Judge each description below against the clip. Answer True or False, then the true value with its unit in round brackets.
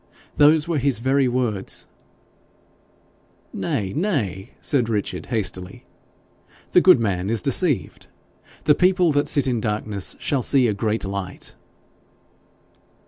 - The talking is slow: True (120 wpm)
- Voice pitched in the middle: False (120 Hz)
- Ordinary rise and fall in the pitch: False (6.1 semitones)